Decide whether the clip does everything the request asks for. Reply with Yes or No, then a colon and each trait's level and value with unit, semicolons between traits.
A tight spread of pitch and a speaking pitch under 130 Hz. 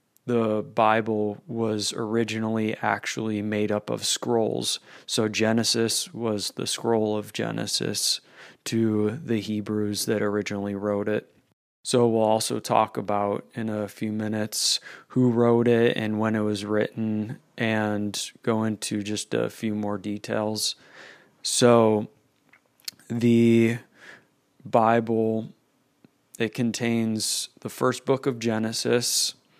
Yes: narrow, 1.6 semitones; low, 110 Hz